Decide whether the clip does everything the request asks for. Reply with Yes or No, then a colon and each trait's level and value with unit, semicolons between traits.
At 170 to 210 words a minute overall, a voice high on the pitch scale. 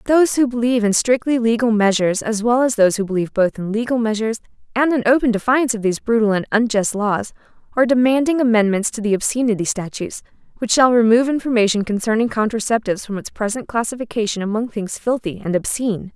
Yes: average, 180 wpm; high, 225 Hz